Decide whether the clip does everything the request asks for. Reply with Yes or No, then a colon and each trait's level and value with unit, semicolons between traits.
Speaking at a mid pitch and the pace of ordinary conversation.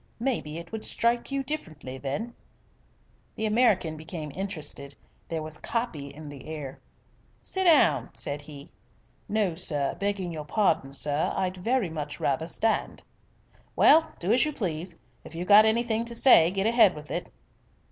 Yes: medium, 180 Hz; average, 155 wpm